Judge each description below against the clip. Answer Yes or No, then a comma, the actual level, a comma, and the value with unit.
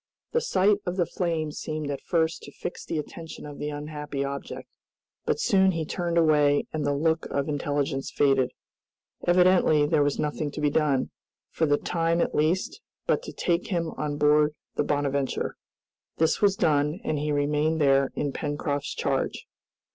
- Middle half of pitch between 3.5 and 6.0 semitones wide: No, narrow, 2.4 semitones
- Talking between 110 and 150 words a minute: No, average, 170 wpm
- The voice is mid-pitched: Yes, medium, 150 Hz